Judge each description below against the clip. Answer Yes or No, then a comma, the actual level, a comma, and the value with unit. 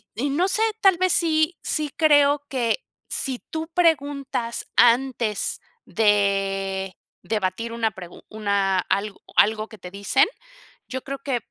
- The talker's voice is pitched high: Yes, high, 235 Hz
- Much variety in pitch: Yes, wide, 6.2 semitones